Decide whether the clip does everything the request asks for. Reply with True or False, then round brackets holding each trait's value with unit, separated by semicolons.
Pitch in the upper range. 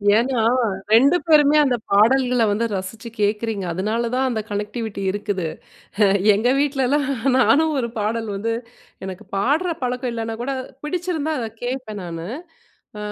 True (235 Hz)